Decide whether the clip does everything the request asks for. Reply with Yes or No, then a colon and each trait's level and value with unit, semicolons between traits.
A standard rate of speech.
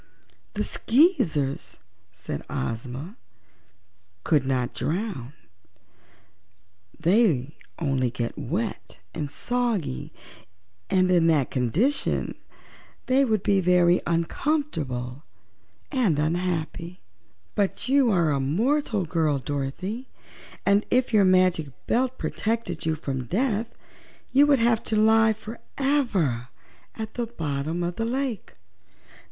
No: slow, 105 wpm